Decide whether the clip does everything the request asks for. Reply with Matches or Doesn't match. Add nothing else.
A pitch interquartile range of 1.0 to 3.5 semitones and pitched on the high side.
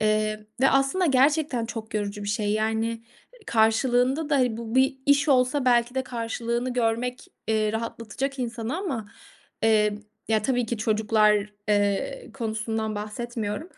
Matches